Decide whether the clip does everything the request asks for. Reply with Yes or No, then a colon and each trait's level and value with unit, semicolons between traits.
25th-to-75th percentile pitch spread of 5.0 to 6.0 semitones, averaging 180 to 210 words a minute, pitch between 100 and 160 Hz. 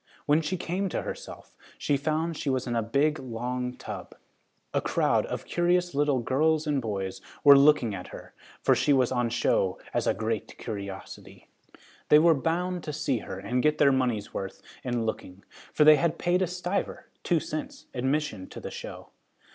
Yes: average, 5.3 semitones; average, 185 wpm; medium, 140 Hz